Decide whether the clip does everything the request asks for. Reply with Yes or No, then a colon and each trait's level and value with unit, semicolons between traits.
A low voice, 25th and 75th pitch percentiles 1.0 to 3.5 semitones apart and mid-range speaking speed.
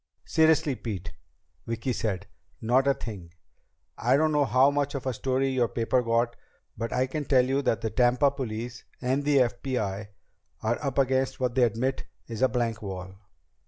Yes: low, 125 Hz; average, 2.8 semitones; average, 175 wpm